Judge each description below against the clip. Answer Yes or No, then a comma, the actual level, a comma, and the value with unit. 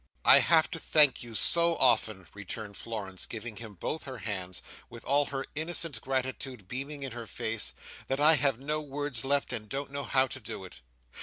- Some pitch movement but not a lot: Yes, average, 4.5 semitones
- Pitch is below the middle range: Yes, low, 130 Hz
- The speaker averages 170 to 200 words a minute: Yes, average, 190 wpm